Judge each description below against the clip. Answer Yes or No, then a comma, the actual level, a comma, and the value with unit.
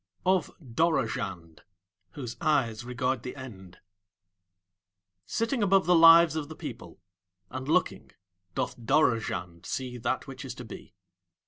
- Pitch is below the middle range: Yes, low, 130 Hz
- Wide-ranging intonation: Yes, wide, 6.4 semitones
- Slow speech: Yes, slow, 125 wpm